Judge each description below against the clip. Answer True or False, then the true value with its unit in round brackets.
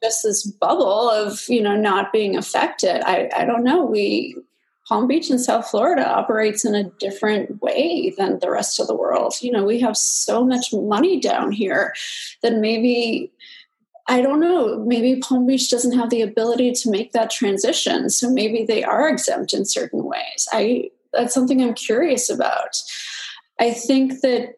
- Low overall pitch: False (235 Hz)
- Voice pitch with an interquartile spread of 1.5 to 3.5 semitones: True (3.1 semitones)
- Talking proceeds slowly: False (175 wpm)